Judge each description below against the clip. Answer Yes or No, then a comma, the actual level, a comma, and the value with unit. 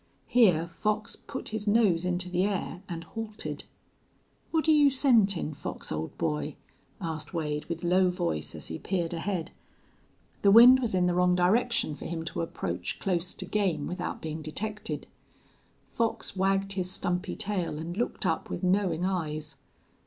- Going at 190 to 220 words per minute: No, average, 160 wpm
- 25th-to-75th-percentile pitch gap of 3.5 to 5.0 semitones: Yes, average, 3.8 semitones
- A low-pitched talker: No, medium, 180 Hz